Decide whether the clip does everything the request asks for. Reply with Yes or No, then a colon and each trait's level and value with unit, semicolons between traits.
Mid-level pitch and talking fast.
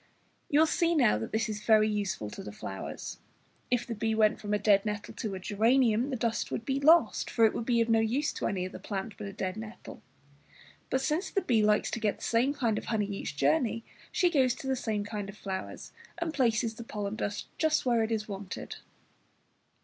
No: high, 220 Hz; fast, 225 wpm